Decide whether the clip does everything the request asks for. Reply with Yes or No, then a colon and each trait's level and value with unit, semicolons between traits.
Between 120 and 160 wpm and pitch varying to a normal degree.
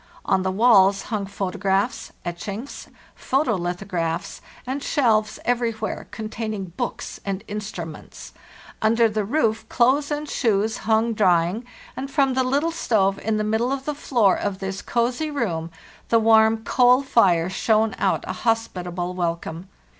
Yes: average, 140 wpm; average, 4.1 semitones